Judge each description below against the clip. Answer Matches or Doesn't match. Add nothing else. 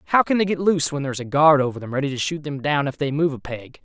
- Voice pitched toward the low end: Doesn't match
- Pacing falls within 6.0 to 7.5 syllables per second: Matches